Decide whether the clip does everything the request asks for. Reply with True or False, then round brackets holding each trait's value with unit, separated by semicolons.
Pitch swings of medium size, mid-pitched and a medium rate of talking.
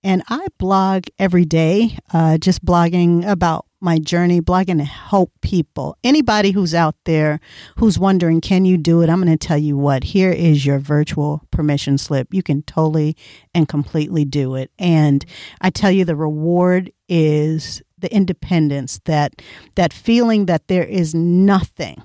True (3.5 semitones; 170 Hz; 165 wpm)